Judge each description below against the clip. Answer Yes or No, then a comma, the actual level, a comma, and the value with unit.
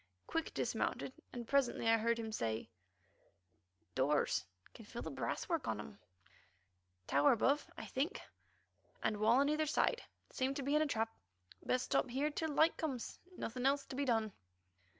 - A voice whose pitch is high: Yes, very high, 255 Hz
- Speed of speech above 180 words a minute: No, average, 165 wpm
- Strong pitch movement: No, average, 4.3 semitones